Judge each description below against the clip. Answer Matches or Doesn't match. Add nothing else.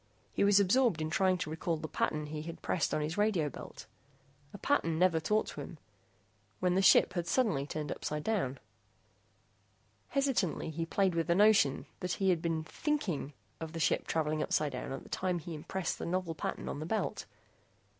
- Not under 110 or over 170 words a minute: Doesn't match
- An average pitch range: Matches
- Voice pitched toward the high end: Doesn't match